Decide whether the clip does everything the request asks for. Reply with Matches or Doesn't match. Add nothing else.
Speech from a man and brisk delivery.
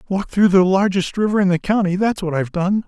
Matches